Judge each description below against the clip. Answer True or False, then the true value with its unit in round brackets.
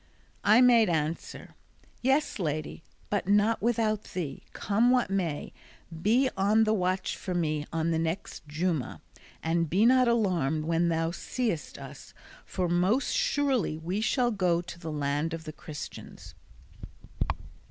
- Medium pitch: True (180 Hz)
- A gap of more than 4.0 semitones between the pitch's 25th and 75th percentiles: True (5.3 semitones)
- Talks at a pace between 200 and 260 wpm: False (140 wpm)